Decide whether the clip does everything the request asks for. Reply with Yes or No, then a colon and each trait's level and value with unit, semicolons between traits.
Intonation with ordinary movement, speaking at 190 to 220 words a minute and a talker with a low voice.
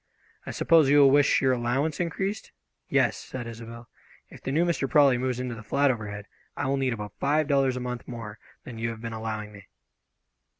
Yes: average, 3.6 semitones; fast, 205 wpm; low, 125 Hz